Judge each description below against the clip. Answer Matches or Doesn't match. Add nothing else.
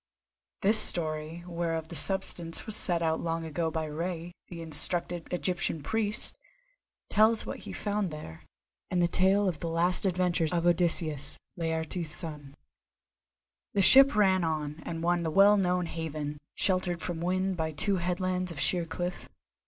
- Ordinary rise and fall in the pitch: Doesn't match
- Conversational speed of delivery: Matches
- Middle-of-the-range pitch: Matches